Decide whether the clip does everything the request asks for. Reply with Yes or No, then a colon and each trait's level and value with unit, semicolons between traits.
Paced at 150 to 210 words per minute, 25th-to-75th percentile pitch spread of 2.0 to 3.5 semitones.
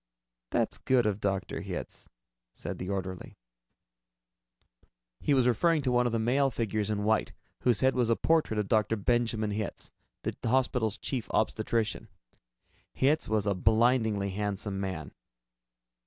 No: average, 140 wpm; average, 3.2 semitones